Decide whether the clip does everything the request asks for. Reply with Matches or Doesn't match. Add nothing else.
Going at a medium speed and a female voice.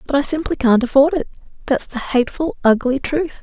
Matches